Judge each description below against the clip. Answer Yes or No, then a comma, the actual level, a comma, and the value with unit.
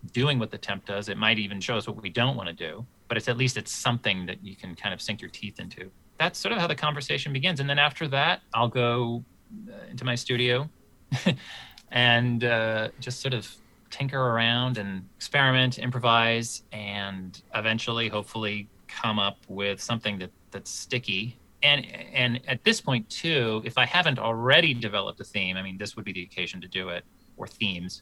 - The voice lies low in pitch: Yes, low, 115 Hz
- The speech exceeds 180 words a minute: Yes, average, 195 wpm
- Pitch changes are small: No, average, 3.9 semitones